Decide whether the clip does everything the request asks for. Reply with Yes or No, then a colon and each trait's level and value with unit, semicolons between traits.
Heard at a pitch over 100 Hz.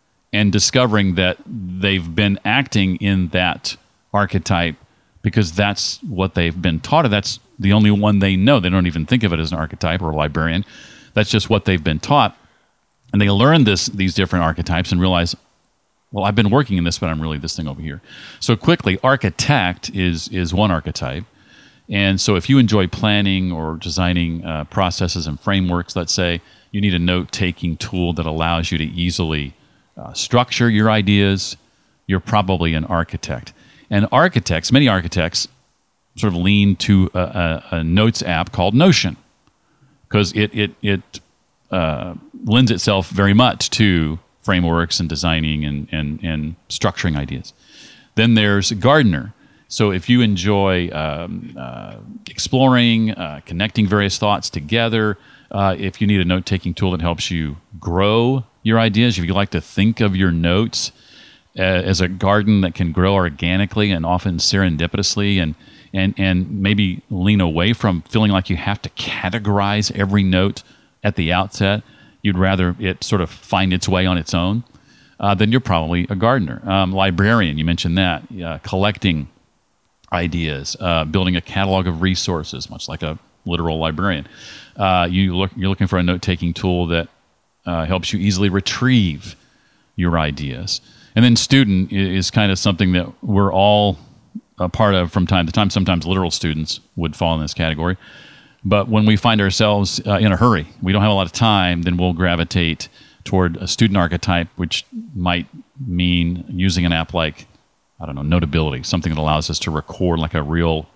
No: very low, 95 Hz